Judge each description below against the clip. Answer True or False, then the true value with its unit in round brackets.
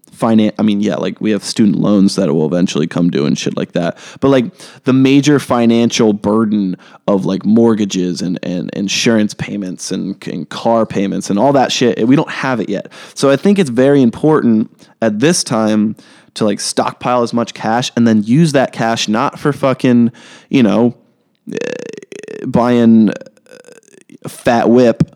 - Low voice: True (115 Hz)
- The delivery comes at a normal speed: True (170 wpm)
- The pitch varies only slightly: False (4.2 semitones)